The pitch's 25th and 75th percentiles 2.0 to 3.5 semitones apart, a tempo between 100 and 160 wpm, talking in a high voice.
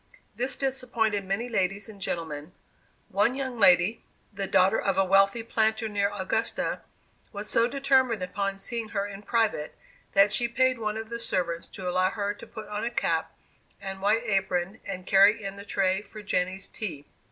No: average, 2.8 semitones; average, 175 wpm; high, 200 Hz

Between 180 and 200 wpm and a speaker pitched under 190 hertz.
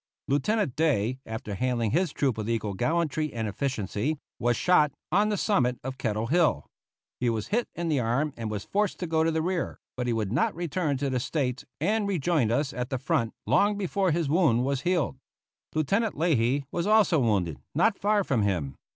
Yes: average, 195 wpm; medium, 140 Hz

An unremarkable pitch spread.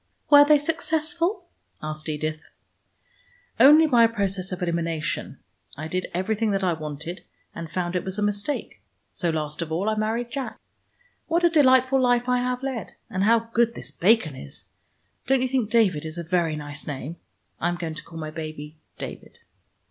No: wide, 7.6 semitones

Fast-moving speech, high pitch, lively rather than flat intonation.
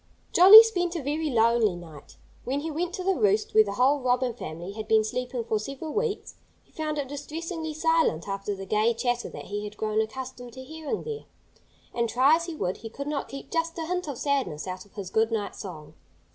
Yes: fast, 220 wpm; very high, 255 Hz; wide, 6.8 semitones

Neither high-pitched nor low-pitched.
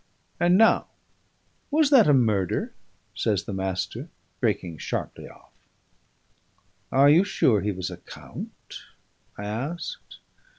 No: low, 115 Hz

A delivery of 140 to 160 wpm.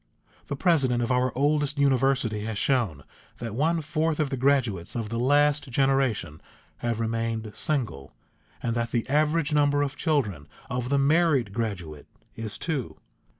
Yes: average, 150 wpm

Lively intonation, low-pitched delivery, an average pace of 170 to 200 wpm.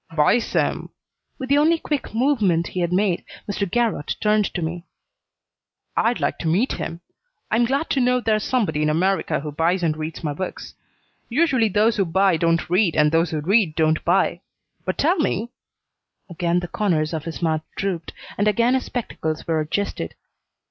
No: wide, 5.9 semitones; medium, 185 Hz; average, 185 wpm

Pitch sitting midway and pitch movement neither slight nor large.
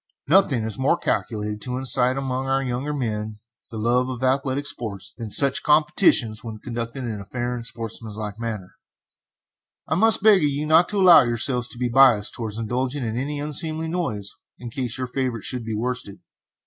No: low, 125 Hz; average, 3.6 semitones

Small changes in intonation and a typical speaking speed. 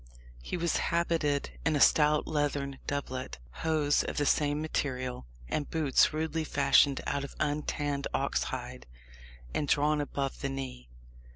Yes: narrow, 1.9 semitones; average, 145 wpm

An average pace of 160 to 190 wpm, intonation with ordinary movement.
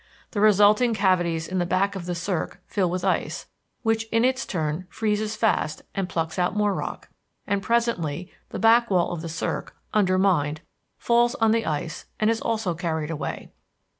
Yes: average, 175 wpm; average, 4.3 semitones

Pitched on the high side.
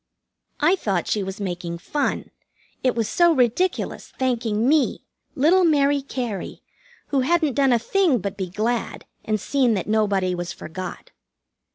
Yes: high, 235 Hz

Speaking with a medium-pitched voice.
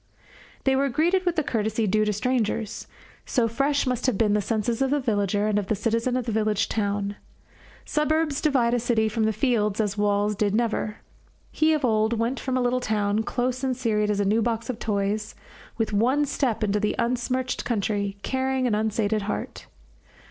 No: high, 225 Hz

